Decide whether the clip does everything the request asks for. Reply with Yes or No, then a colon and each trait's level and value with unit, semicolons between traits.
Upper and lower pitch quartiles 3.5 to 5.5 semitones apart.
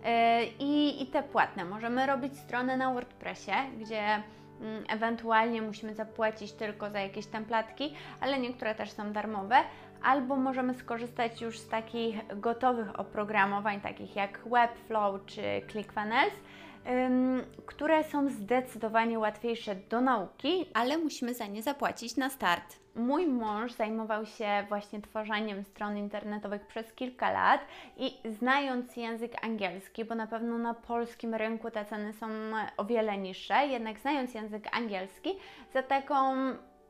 No: average, 3.1 semitones